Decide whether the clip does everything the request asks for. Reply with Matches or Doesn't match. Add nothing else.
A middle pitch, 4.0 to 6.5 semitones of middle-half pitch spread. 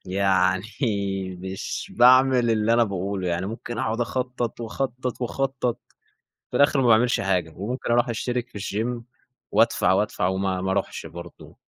Doesn't match